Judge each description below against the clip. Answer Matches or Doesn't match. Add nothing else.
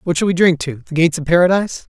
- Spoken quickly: Matches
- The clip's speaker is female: Doesn't match